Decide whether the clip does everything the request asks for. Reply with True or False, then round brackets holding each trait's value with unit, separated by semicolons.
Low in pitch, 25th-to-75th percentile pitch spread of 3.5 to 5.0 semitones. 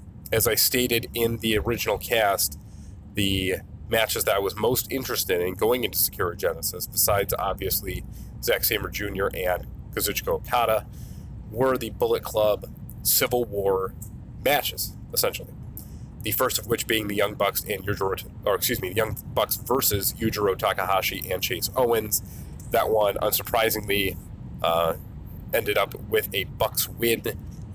True (110 Hz; 3.8 semitones)